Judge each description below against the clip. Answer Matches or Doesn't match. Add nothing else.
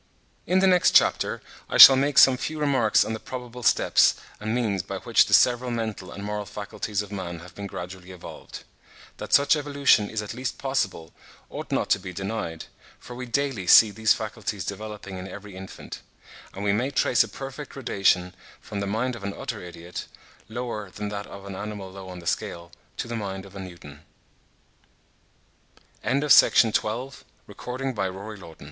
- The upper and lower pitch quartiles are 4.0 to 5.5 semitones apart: Matches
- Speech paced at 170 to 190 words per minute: Matches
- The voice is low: Matches